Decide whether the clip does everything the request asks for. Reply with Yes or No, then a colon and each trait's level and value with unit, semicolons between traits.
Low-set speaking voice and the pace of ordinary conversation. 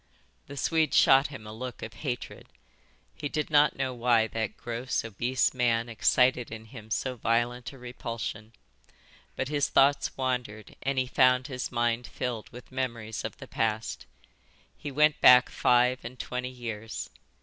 Yes: low, 125 Hz; average, 160 wpm